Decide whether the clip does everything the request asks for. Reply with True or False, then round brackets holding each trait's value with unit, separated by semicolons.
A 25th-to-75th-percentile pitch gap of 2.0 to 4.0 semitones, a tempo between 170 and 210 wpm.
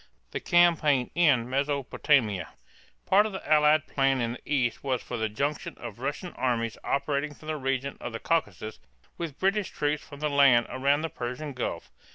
True (3.7 semitones; 180 wpm)